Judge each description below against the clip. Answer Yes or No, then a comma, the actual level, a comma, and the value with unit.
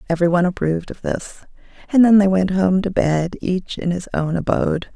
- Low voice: No, medium, 180 Hz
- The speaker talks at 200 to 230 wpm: Yes, fast, 205 wpm